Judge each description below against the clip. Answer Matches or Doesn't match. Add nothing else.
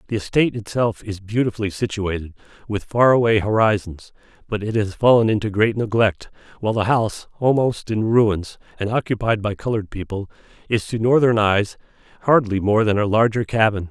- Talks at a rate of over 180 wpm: Doesn't match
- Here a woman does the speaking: Doesn't match